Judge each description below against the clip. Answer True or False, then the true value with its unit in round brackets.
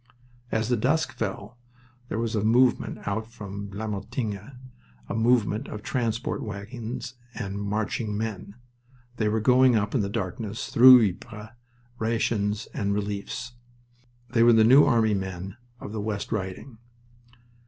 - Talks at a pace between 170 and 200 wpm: False (140 wpm)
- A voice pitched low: True (110 Hz)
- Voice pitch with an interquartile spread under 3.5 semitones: True (2.4 semitones)